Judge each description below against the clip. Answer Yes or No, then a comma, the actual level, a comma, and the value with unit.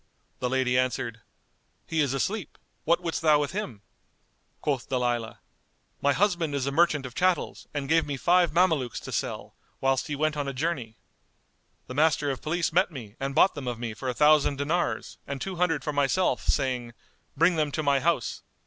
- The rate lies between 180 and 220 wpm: Yes, average, 190 wpm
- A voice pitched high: No, medium, 145 Hz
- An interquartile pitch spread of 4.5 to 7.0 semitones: No, average, 4.1 semitones